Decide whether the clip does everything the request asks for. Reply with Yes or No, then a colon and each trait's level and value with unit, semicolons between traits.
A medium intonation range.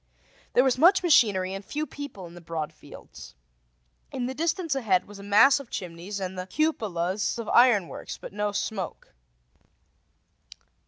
No: wide, 6.5 semitones